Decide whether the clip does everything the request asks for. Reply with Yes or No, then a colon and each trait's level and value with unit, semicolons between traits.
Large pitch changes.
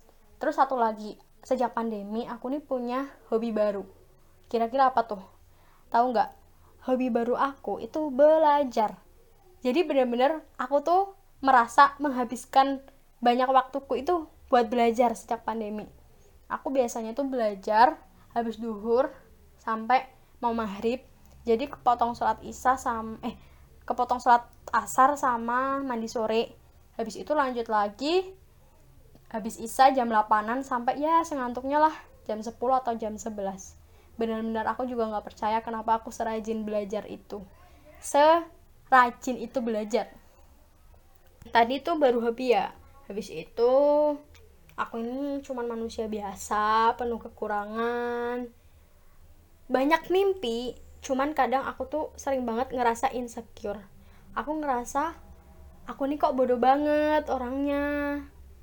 No: average, 3.2 semitones